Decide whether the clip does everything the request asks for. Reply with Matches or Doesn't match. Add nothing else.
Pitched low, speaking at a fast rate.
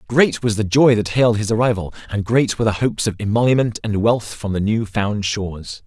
Matches